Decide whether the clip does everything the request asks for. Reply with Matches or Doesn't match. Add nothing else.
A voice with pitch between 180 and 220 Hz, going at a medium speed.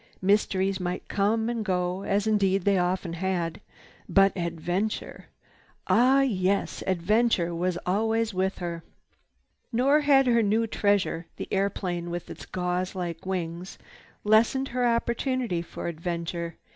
Doesn't match